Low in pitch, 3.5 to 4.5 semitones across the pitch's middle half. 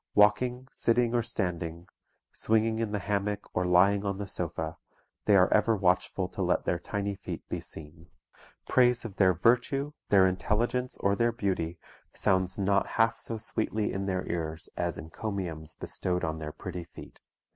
Yes: low, 100 Hz; average, 3.9 semitones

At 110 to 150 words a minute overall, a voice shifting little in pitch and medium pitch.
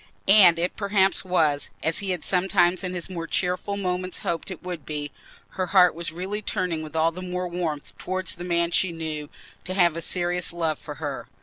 No: average, 200 wpm; narrow, 2.1 semitones; medium, 175 Hz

